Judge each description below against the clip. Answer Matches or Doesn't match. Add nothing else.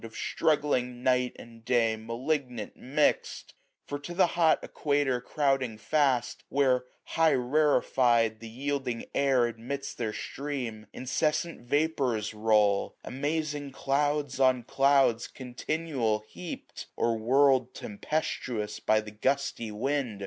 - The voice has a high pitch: Doesn't match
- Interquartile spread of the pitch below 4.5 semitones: Matches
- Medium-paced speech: Doesn't match